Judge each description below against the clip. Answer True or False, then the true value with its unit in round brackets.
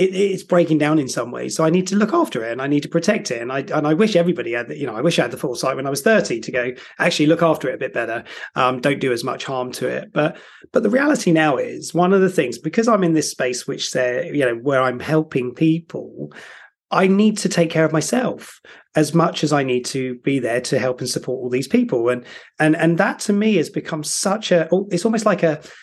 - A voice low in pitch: False (160 Hz)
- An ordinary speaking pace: False (270 wpm)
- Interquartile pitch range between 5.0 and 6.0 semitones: True (5.6 semitones)